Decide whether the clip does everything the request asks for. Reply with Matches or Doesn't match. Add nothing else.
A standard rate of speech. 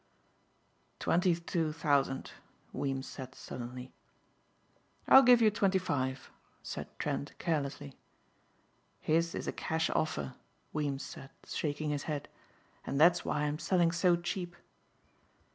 Doesn't match